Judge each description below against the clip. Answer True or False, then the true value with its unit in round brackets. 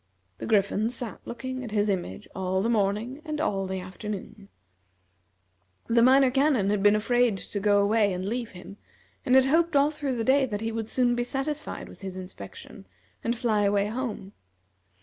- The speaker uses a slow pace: False (185 wpm)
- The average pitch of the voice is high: True (225 Hz)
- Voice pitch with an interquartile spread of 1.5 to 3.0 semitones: False (4.3 semitones)